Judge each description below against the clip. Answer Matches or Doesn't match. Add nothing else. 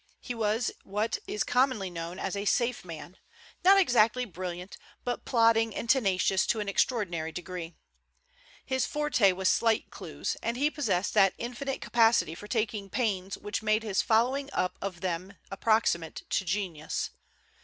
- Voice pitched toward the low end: Doesn't match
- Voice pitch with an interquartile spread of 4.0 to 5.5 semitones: Matches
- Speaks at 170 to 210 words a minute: Doesn't match